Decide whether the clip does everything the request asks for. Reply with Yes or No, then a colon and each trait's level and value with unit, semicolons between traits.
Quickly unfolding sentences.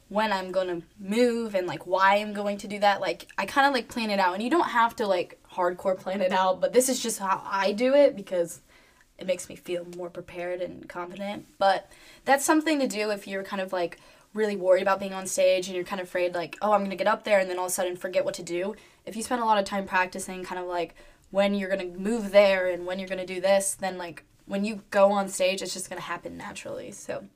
Yes: fast, 265 wpm